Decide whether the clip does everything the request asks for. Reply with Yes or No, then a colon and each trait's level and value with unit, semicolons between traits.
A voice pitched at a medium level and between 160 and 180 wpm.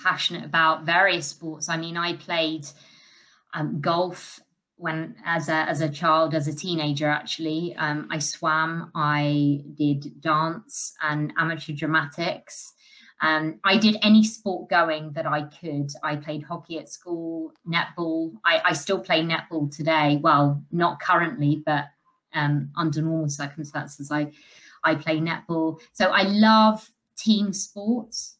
No: medium, 160 Hz; average, 140 wpm